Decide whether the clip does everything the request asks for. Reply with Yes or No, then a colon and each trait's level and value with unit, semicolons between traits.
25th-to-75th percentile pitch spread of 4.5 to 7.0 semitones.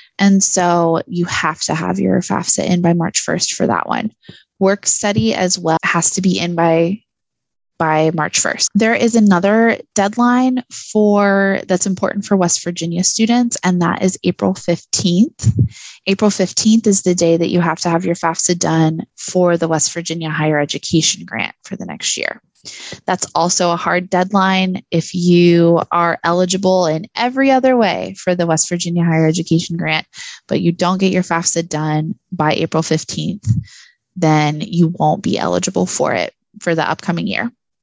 No: average, 2.8 semitones